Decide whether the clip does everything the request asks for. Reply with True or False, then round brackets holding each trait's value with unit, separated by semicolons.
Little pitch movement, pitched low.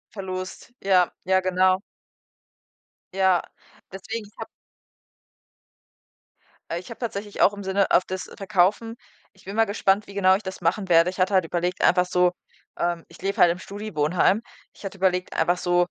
False (1.8 semitones; 185 Hz)